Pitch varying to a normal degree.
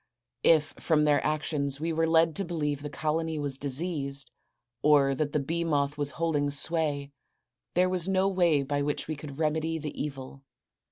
No: narrow, 2.3 semitones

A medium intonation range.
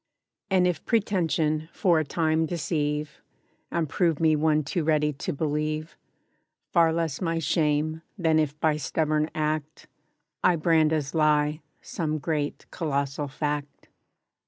No: narrow, 1.5 semitones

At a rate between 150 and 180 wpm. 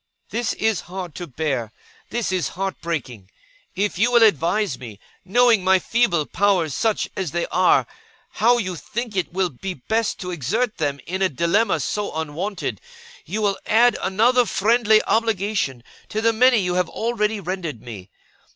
Yes: average, 165 wpm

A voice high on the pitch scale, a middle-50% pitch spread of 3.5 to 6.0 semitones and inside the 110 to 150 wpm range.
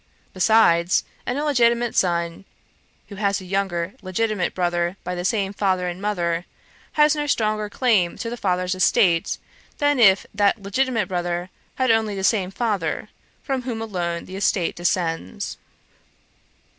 Yes: high, 195 Hz; average, 4.1 semitones; average, 145 wpm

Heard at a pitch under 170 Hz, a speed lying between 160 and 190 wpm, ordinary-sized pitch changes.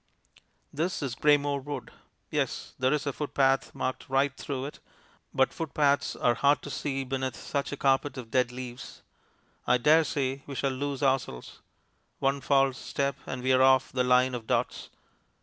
No: low, 135 Hz; average, 170 wpm; narrow, 1.6 semitones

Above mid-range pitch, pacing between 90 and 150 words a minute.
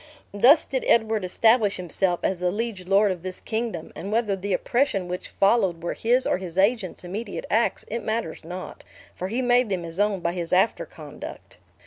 No: high, 195 Hz; average, 190 wpm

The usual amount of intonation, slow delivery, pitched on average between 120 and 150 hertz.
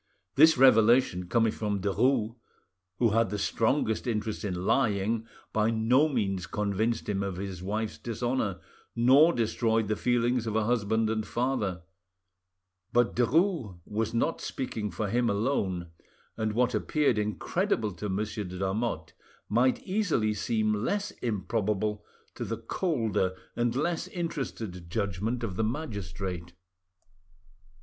No: average, 3.3 semitones; slow, 130 wpm; low, 110 Hz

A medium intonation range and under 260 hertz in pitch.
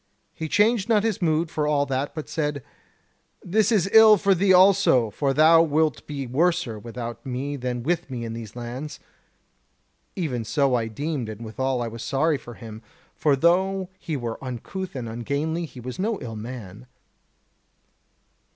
No: wide, 6.2 semitones; medium, 140 Hz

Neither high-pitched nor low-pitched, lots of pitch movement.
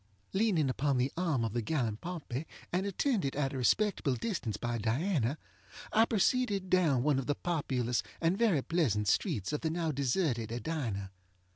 Yes: medium, 145 Hz; wide, 6.7 semitones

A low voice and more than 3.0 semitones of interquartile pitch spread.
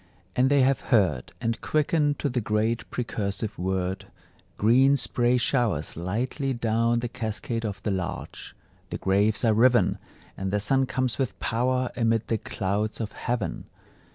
Yes: low, 115 Hz; average, 3.5 semitones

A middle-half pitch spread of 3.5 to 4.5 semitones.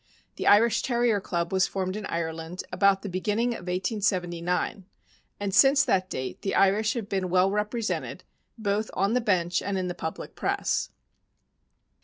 No: average, 2.7 semitones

